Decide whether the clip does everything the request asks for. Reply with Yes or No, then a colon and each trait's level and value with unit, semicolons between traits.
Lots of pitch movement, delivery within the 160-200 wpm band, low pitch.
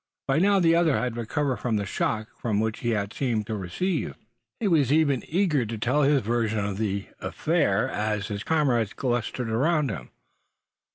Yes: wide, 5.7 semitones; average, 175 wpm; low, 120 Hz